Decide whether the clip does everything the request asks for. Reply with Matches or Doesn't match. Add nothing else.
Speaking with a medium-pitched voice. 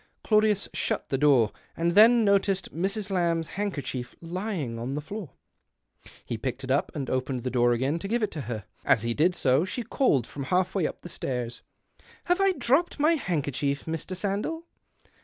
Matches